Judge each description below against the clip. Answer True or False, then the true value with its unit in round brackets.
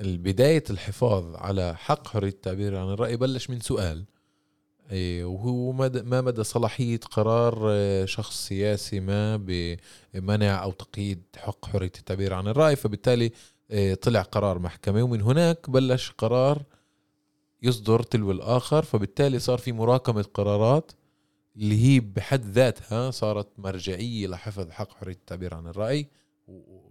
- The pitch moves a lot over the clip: False (4.2 semitones)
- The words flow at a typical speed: True (125 wpm)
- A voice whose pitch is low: True (105 Hz)